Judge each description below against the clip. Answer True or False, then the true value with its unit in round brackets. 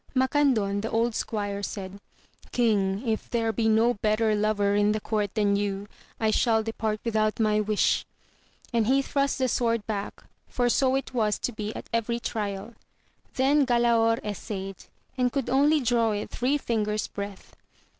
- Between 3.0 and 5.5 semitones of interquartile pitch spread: False (2.6 semitones)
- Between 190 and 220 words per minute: False (165 wpm)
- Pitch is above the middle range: True (220 Hz)